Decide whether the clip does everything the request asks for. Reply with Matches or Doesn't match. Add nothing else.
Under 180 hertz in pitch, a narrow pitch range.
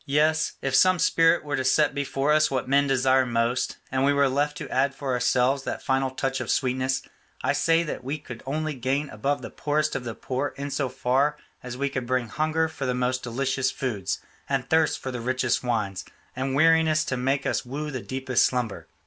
Matches